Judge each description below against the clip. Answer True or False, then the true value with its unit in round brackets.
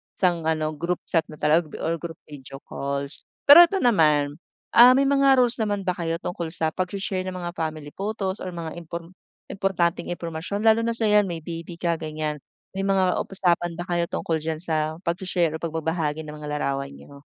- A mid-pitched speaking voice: True (170 Hz)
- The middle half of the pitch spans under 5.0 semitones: True (3.6 semitones)